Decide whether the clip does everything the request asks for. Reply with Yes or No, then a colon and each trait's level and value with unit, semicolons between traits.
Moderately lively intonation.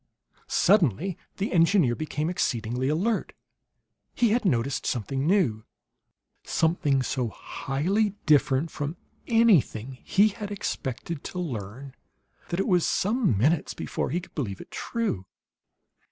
No: wide, 7.1 semitones